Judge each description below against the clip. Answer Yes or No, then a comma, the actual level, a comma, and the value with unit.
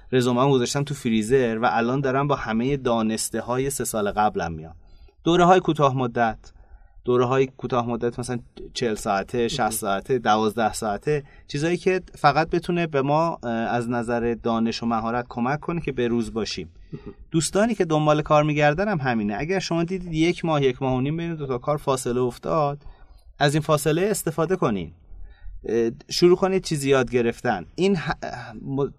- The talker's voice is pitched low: Yes, low, 130 Hz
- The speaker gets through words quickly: Yes, fast, 170 wpm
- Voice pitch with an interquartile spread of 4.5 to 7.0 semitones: Yes, average, 4.9 semitones